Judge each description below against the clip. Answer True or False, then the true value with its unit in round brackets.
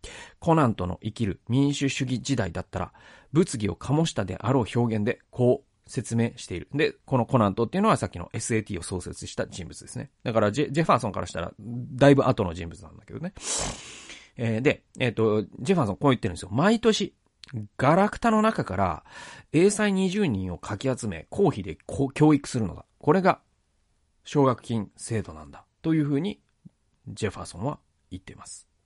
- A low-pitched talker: True (115 Hz)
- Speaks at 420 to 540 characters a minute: False (370 characters per minute)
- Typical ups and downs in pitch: False (5.8 semitones)